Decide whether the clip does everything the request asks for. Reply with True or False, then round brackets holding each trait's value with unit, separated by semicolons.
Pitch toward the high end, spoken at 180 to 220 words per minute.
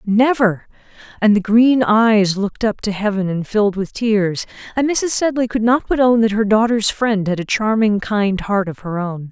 True (215 Hz; 205 wpm)